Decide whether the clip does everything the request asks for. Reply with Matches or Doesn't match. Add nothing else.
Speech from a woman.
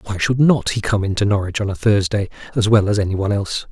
Doesn't match